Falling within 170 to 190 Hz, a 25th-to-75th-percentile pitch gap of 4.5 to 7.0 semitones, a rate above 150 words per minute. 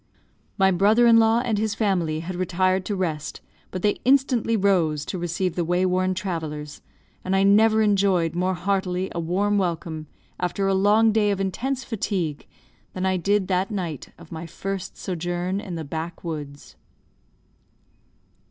No: medium, 185 Hz; average, 3.1 semitones; average, 160 wpm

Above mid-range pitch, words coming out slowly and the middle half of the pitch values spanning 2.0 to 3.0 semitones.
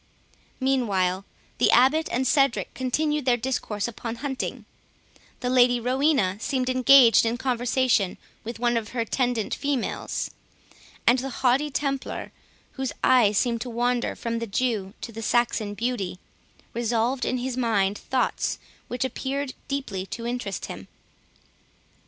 Yes: high, 245 Hz; slow, 130 wpm; narrow, 2.5 semitones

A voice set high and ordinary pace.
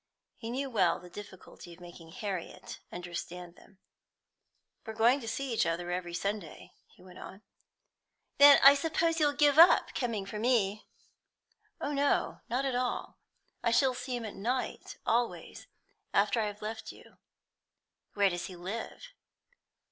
Yes: high, 220 Hz; average, 155 wpm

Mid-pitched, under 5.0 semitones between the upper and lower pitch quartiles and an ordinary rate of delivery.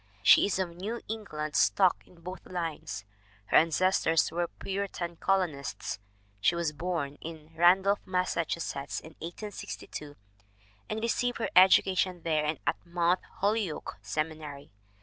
No: medium, 170 Hz; average, 3.5 semitones; slow, 130 wpm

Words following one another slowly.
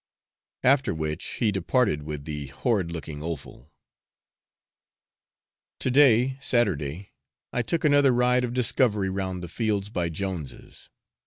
Yes: slow, 120 wpm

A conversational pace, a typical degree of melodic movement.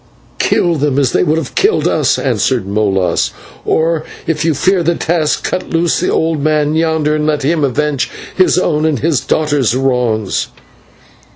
Yes: average, 170 wpm; average, 3.3 semitones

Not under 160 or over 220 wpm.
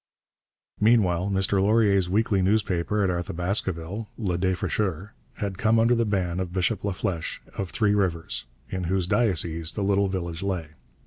No: average, 145 wpm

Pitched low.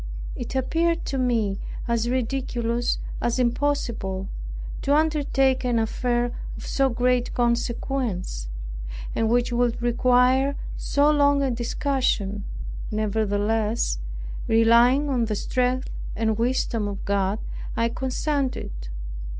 No: high, 240 Hz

